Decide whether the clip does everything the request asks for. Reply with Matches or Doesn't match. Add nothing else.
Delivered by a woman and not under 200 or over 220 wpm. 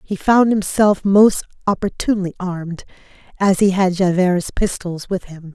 Doesn't match